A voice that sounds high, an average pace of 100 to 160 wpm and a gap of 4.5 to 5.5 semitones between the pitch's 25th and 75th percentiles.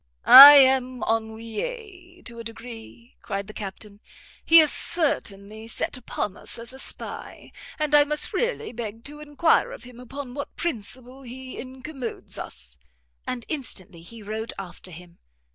Yes: high, 245 Hz; average, 155 wpm; average, 5.0 semitones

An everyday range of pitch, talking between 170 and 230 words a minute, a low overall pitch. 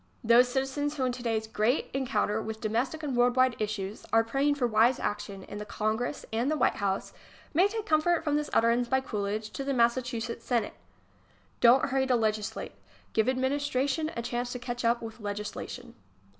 No: average, 3.3 semitones; average, 190 wpm; high, 245 Hz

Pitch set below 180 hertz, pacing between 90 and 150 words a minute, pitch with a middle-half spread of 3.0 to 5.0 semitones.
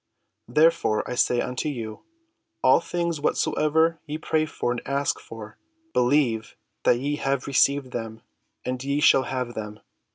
Yes: low, 135 Hz; average, 140 wpm; average, 3.8 semitones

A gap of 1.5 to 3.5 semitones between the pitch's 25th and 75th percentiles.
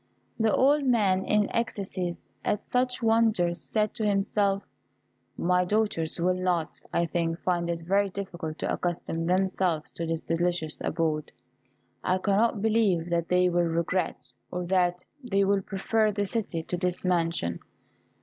Yes: average, 3.1 semitones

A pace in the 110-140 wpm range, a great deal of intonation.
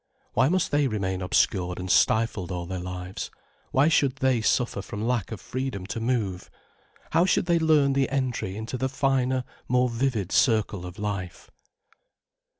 No: average, 160 wpm; wide, 5.9 semitones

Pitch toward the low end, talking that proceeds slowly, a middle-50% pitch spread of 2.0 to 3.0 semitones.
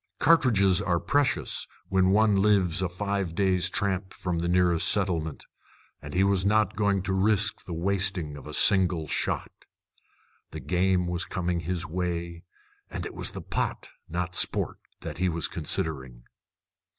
No: very low, 90 Hz; average, 155 wpm; narrow, 2.4 semitones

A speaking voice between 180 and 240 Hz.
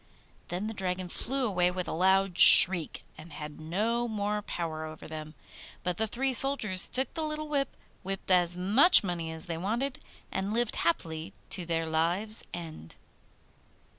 Yes: medium, 185 Hz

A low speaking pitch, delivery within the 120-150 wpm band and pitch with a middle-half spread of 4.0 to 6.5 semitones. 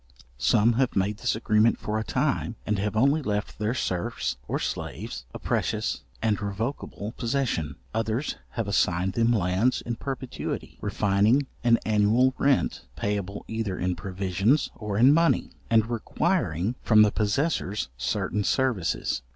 No: low, 110 Hz; average, 145 wpm; average, 3.2 semitones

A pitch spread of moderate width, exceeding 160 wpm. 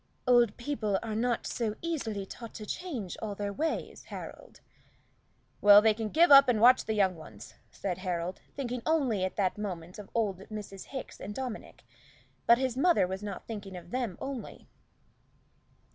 Yes: average, 4.3 semitones; average, 170 wpm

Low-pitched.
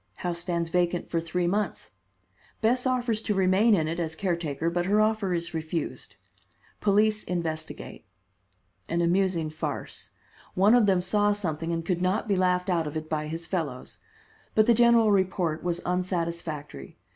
No: medium, 180 Hz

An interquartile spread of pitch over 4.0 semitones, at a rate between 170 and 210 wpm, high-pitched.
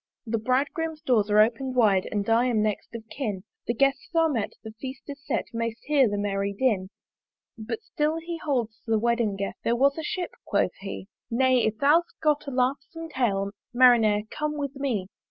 Yes: average, 4.6 semitones; average, 190 wpm; high, 245 Hz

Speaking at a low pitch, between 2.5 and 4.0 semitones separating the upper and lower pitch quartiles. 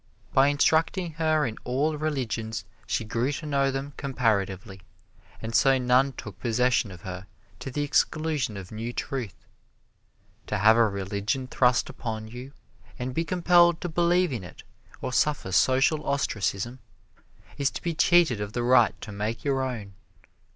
No: low, 125 Hz; average, 5.0 semitones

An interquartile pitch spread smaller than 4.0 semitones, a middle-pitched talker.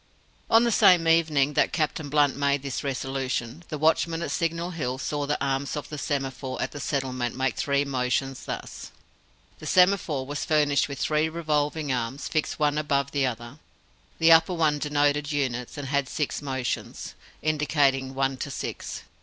Yes: narrow, 2.5 semitones; medium, 145 Hz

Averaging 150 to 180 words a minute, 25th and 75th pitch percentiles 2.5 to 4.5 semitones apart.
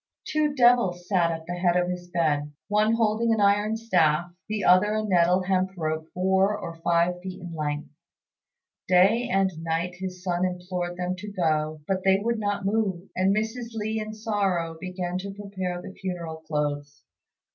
Yes: average, 175 wpm; average, 3.1 semitones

